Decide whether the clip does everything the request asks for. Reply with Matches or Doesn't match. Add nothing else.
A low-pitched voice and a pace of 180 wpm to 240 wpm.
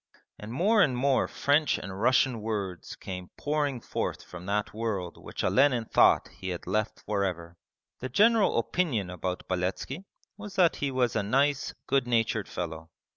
Doesn't match